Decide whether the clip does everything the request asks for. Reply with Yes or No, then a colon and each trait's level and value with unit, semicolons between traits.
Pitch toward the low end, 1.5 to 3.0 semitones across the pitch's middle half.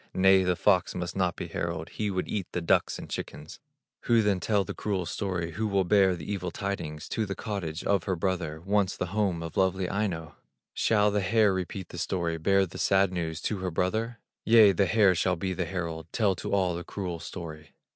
Yes: very low, 95 Hz; average, 2.7 semitones